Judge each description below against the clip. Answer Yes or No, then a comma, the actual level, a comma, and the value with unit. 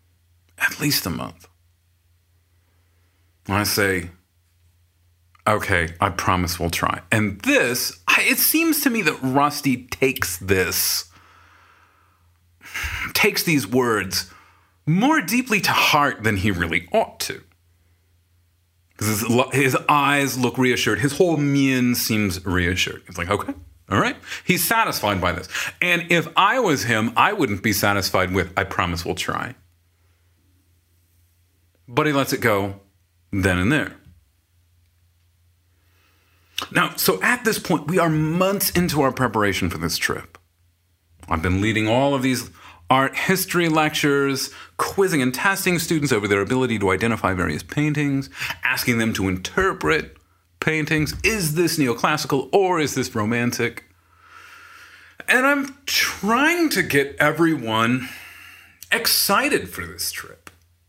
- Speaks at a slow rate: Yes, slow, 130 wpm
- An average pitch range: No, wide, 8.8 semitones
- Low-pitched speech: Yes, low, 105 Hz